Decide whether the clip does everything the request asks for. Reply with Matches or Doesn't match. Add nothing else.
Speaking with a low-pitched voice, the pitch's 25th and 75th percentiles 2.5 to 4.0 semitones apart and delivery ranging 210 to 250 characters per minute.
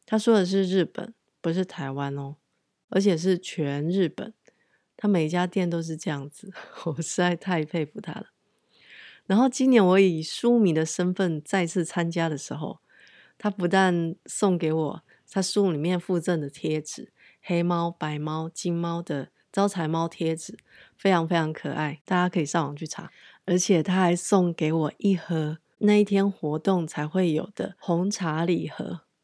Doesn't match